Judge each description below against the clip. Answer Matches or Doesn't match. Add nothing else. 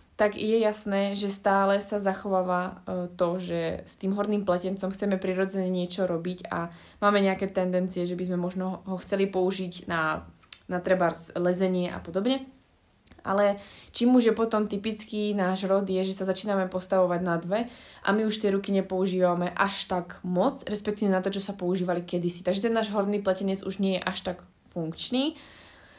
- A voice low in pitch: Doesn't match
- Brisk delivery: Matches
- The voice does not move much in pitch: Matches